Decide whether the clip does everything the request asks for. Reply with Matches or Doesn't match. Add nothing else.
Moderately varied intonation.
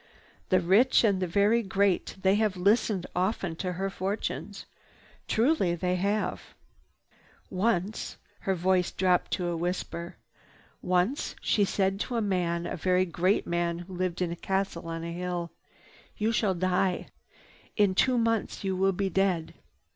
Doesn't match